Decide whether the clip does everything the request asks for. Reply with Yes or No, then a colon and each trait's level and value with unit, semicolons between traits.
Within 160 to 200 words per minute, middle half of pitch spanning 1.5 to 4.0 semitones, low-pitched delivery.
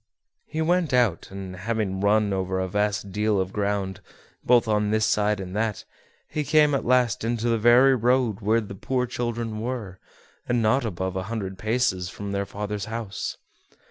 Yes: average, 175 wpm; average, 3.4 semitones; low, 110 Hz